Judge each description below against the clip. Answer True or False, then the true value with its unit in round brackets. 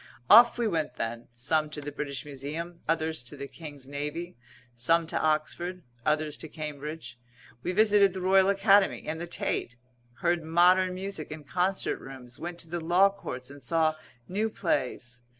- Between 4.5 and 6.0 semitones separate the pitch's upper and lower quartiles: False (4.1 semitones)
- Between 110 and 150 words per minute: False (170 wpm)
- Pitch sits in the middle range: True (160 Hz)